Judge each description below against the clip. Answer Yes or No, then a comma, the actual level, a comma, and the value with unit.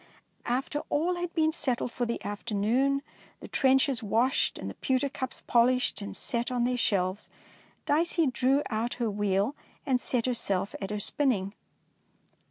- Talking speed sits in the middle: Yes, average, 155 wpm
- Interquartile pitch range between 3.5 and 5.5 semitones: Yes, average, 4.2 semitones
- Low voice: No, high, 245 Hz